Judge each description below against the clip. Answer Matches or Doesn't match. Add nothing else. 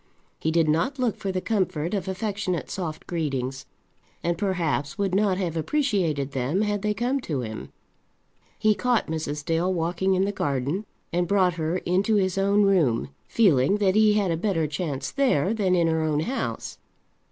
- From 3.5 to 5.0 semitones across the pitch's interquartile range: Matches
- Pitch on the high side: Doesn't match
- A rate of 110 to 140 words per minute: Doesn't match